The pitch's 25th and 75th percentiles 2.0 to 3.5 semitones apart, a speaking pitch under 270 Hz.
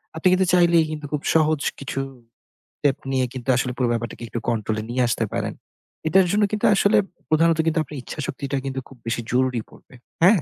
No: average, 4.5 semitones; medium, 140 Hz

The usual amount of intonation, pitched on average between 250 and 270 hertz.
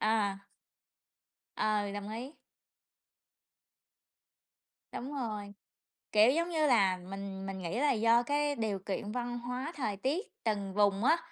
No: average, 4.3 semitones; high, 220 Hz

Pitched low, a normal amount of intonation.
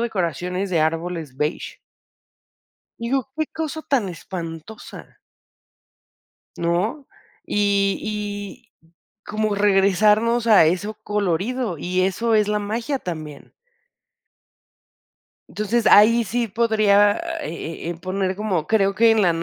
No: high, 205 Hz; average, 3.7 semitones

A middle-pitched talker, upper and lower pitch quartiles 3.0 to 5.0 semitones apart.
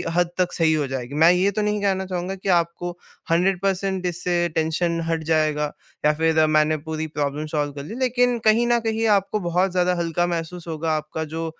Yes: medium, 170 Hz; average, 3.3 semitones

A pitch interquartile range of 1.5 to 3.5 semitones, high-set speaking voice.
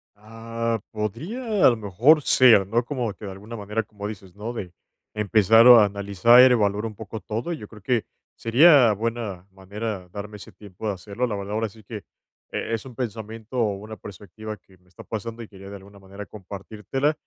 No: narrow, 2.5 semitones; low, 110 Hz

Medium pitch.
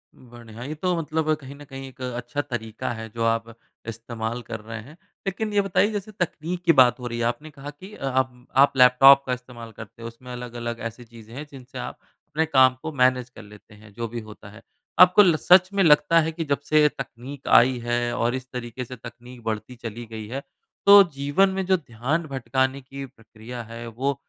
No: low, 125 Hz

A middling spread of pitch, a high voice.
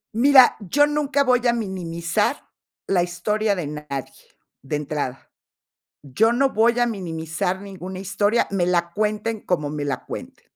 No: wide, 5.8 semitones; high, 195 Hz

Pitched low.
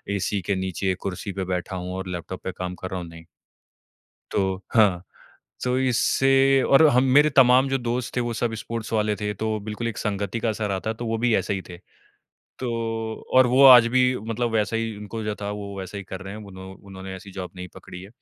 Yes: low, 105 Hz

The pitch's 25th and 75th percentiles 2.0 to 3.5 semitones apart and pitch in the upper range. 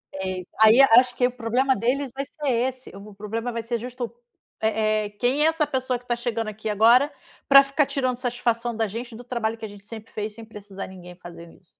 Yes: average, 2.9 semitones; high, 235 Hz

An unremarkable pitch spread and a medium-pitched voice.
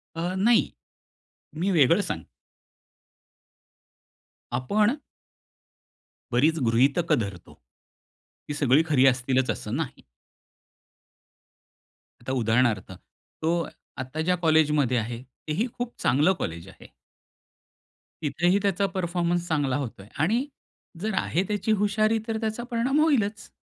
No: wide, 7.9 semitones; medium, 160 Hz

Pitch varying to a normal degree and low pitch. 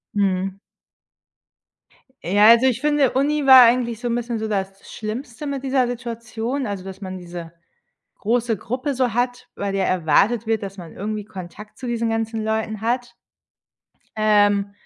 No: average, 3.6 semitones; high, 225 Hz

